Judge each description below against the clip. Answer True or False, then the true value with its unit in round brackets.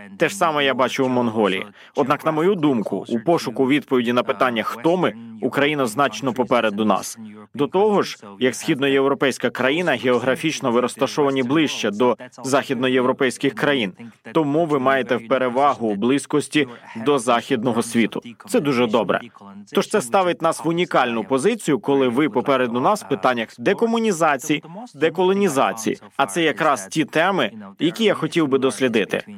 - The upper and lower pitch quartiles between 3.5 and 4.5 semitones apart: True (4.2 semitones)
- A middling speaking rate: True (145 wpm)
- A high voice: False (135 Hz)